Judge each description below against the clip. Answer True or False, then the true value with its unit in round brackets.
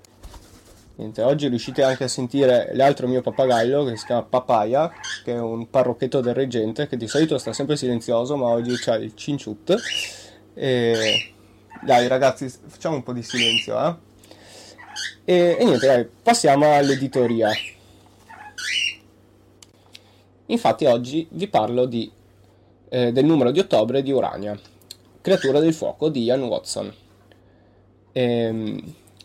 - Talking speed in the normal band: True (130 wpm)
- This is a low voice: True (120 Hz)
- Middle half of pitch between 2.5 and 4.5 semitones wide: True (4.2 semitones)